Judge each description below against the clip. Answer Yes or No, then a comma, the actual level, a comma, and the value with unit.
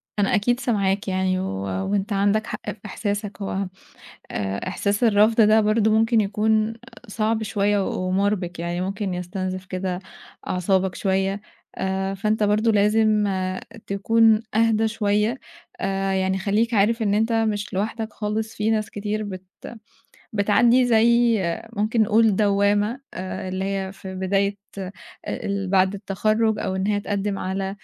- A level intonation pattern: Yes, narrow, 2.2 semitones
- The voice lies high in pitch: Yes, high, 205 Hz